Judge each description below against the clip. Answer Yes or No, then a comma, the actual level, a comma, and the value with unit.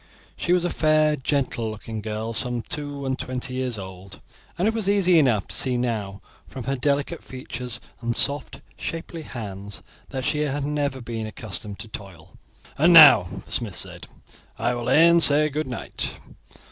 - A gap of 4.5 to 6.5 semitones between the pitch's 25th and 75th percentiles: Yes, average, 5.0 semitones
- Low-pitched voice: Yes, low, 130 Hz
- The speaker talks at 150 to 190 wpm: Yes, average, 170 wpm